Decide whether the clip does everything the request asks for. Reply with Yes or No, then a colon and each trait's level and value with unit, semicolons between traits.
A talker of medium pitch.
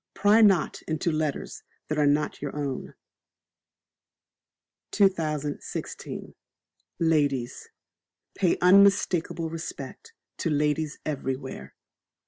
Yes: medium, 155 Hz